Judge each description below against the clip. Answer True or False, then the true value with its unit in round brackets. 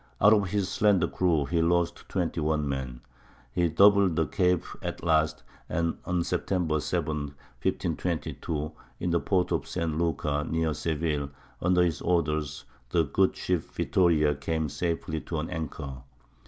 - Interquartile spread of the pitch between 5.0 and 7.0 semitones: False (2.7 semitones)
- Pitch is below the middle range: True (80 Hz)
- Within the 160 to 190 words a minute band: False (145 wpm)